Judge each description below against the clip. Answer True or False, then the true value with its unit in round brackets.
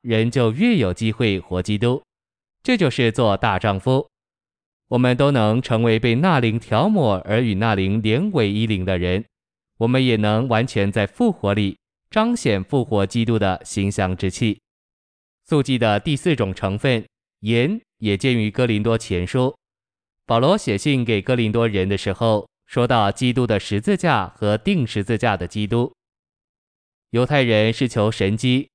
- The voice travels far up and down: False (3.9 semitones)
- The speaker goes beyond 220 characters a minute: True (230 characters per minute)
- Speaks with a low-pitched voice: True (115 Hz)